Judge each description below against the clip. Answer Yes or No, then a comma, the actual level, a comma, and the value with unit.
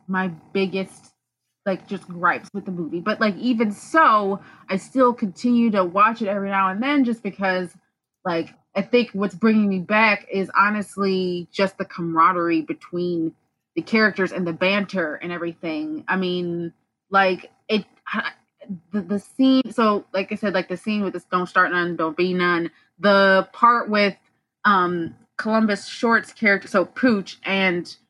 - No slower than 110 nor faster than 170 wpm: Yes, average, 160 wpm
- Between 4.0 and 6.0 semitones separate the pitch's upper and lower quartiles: No, average, 3.2 semitones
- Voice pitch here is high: Yes, high, 195 Hz